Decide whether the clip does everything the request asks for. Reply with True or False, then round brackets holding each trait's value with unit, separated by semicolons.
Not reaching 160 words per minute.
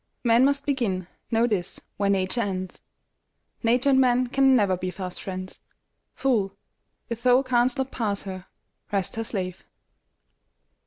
True (145 wpm)